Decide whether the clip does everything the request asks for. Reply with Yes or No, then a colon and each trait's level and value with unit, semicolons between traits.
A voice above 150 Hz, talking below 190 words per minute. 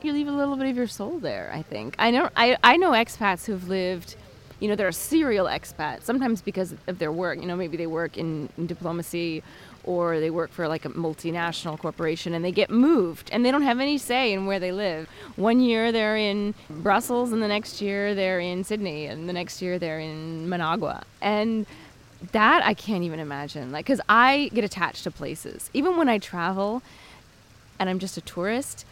No: medium, 185 Hz; fast, 205 wpm